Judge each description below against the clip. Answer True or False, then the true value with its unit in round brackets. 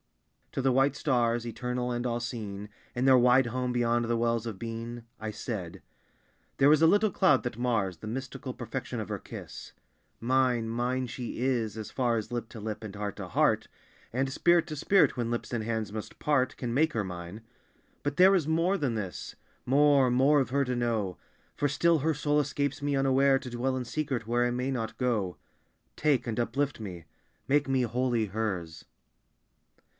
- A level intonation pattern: False (3.1 semitones)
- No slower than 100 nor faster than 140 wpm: False (190 wpm)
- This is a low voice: True (125 Hz)